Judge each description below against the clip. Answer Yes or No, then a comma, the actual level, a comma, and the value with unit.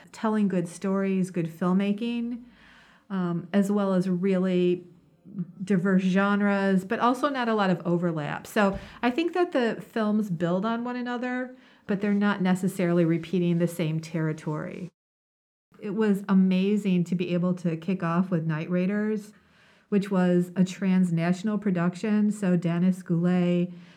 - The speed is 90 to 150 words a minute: Yes, average, 145 wpm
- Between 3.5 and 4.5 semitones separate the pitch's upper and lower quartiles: No, average, 2.8 semitones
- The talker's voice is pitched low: No, high, 190 Hz